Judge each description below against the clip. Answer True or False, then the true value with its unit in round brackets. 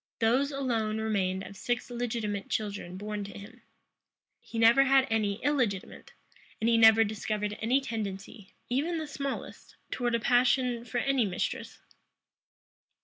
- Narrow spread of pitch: False (3.2 semitones)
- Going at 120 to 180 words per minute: True (140 wpm)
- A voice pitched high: True (225 Hz)